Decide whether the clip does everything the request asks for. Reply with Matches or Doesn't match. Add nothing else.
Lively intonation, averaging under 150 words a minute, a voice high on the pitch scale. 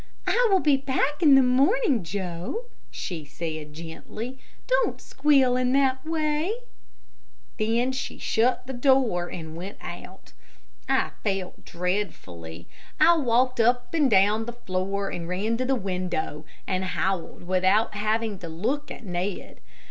Matches